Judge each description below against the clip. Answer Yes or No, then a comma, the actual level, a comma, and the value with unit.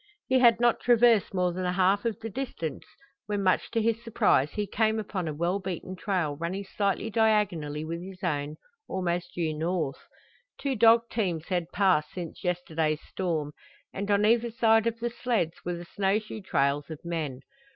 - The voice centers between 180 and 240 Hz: Yes, medium, 185 Hz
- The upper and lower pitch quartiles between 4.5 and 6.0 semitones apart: Yes, average, 4.9 semitones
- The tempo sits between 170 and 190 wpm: Yes, average, 180 wpm